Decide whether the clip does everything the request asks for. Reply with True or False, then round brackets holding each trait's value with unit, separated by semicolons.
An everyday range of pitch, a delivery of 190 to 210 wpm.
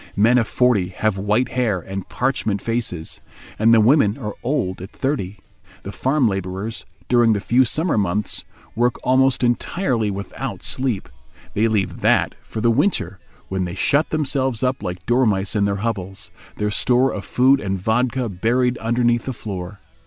False (4.2 semitones; 165 wpm)